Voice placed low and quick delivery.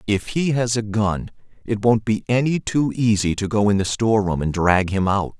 Yes: low, 105 Hz; fast, 220 wpm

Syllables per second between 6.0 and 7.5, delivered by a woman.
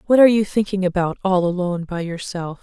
Yes: 6.2 syllables/s; female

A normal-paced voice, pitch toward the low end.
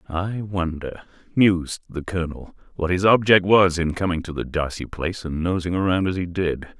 Yes: average, 185 wpm; very low, 90 Hz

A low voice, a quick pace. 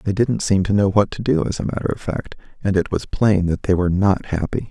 Yes: low, 100 Hz; fast, 280 wpm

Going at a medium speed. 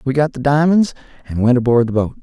No: fast, 245 wpm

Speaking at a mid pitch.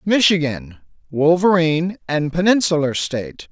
Yes: medium, 170 Hz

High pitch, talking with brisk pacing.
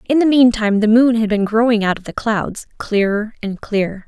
Yes: high, 220 Hz; fast, 235 wpm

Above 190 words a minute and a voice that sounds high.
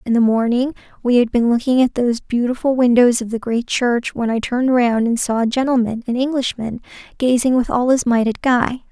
Yes: average, 200 wpm; high, 240 Hz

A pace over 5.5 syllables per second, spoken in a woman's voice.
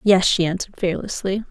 Yes: 6.0 syllables/s; female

